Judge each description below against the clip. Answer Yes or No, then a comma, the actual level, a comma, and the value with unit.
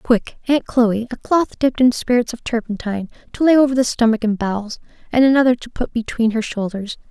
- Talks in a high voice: Yes, high, 235 Hz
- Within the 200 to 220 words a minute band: Yes, fast, 205 wpm